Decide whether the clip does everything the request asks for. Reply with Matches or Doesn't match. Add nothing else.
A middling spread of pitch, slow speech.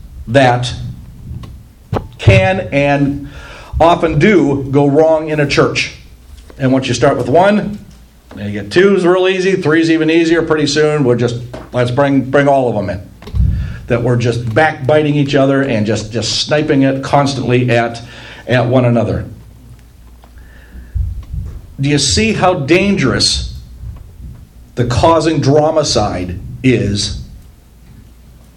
Doesn't match